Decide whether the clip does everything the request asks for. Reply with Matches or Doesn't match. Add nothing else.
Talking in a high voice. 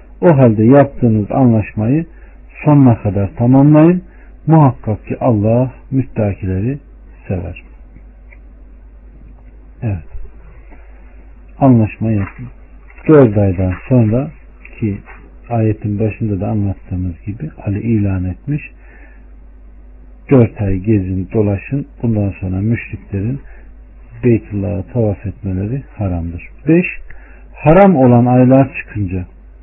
Doesn't match